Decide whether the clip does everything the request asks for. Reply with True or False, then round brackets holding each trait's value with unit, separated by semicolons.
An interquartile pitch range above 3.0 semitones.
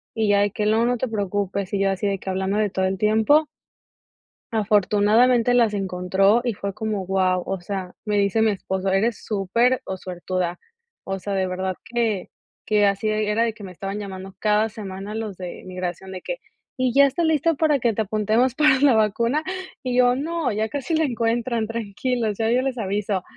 True (3.6 semitones)